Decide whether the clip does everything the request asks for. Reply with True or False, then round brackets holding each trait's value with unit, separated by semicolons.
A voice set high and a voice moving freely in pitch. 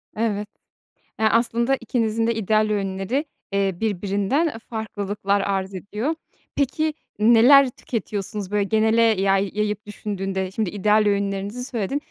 False (210 Hz; 2.5 semitones)